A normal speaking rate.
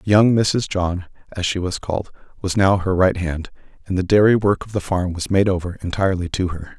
No: fast, 220 wpm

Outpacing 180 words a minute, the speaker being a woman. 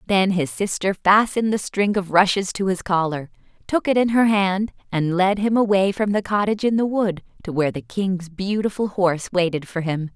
Yes: fast, 205 wpm; female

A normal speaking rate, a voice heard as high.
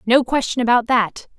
Yes: average, 175 wpm; high, 240 Hz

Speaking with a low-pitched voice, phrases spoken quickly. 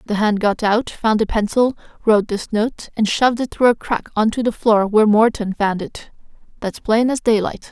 No: high, 220 Hz; fast, 220 wpm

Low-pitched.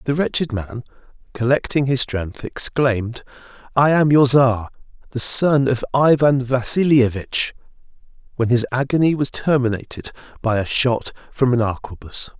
Yes: low, 125 Hz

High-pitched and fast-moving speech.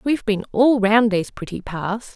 Yes: high, 215 Hz; fast, 220 wpm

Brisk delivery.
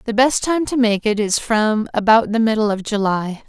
Yes: fast, 225 wpm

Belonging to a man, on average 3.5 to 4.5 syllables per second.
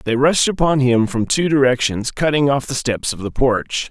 No: male; 4.8 syllables/s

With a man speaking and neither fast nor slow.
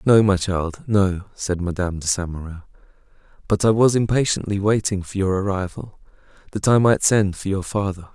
Yes: male; average, 175 wpm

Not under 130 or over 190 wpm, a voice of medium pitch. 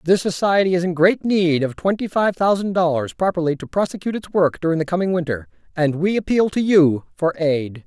No: fast, 205 wpm; medium, 175 Hz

